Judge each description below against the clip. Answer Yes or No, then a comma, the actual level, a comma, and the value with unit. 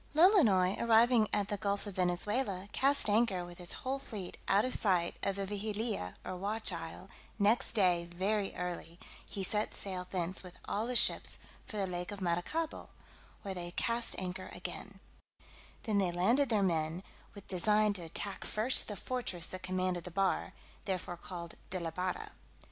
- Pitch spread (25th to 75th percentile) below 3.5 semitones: Yes, average, 3.1 semitones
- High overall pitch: Yes, high, 195 Hz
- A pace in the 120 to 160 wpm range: No, average, 170 wpm